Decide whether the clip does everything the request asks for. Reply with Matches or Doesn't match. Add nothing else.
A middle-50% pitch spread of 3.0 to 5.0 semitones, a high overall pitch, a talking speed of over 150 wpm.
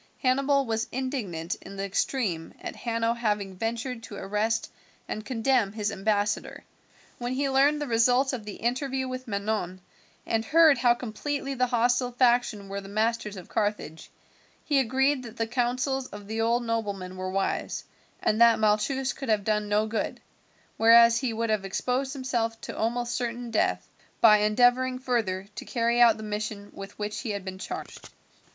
Matches